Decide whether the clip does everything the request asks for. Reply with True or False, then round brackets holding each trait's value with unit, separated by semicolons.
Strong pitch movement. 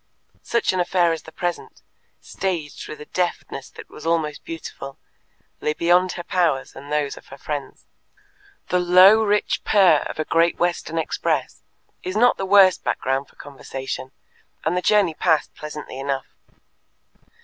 False (3.7 semitones)